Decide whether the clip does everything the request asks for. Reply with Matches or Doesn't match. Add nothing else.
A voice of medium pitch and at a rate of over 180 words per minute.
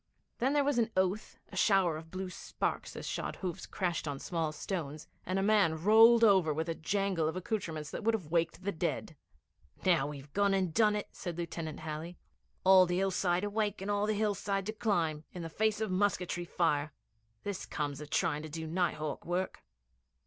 Matches